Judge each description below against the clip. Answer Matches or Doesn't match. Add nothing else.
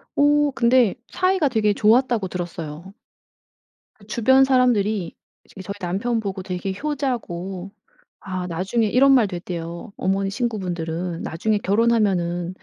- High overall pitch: Matches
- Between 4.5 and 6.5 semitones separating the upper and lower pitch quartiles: Matches